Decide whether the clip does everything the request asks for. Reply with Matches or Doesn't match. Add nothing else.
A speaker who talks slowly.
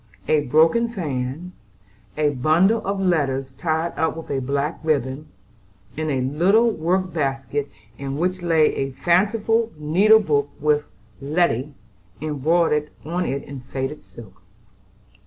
Matches